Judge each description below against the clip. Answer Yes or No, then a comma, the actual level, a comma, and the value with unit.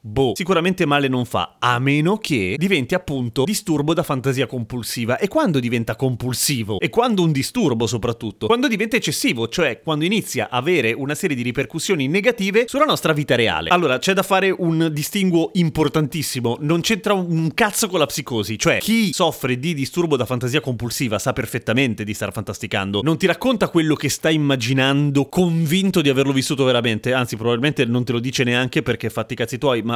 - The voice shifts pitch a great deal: Yes, wide, 5.7 semitones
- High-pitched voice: No, medium, 140 Hz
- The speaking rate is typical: No, fast, 185 wpm